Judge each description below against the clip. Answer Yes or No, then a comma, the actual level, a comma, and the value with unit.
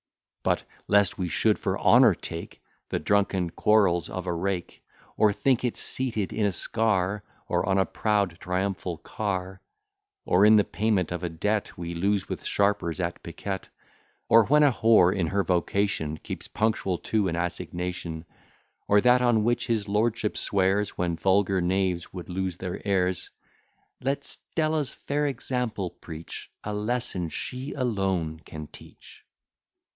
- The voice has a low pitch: Yes, low, 100 Hz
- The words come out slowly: No, average, 150 wpm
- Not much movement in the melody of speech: No, average, 3.5 semitones